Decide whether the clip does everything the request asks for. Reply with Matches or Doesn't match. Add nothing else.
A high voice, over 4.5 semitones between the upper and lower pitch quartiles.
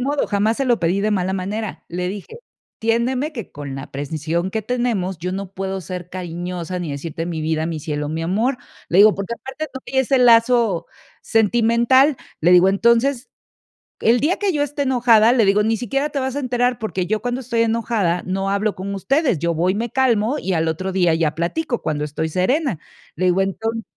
Matches